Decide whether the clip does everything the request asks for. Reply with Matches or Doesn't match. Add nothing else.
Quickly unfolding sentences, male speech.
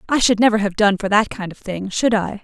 Doesn't match